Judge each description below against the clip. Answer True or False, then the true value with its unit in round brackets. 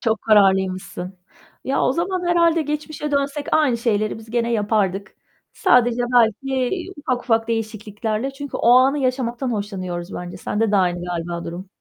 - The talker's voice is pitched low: False (225 Hz)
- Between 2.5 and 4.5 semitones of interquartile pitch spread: False (5.1 semitones)